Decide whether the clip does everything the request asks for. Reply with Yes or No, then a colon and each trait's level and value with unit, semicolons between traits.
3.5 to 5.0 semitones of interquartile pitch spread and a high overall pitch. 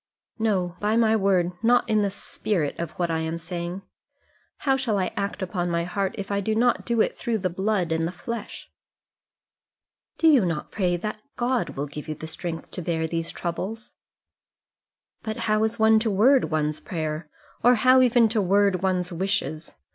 Yes: average, 4.4 semitones; high, 195 Hz